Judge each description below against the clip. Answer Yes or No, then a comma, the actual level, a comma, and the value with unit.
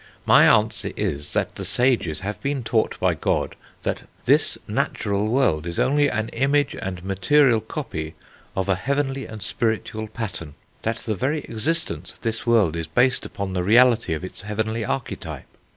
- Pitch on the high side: No, low, 110 Hz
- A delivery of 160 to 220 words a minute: Yes, average, 170 wpm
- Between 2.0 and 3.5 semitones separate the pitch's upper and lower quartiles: No, average, 5.2 semitones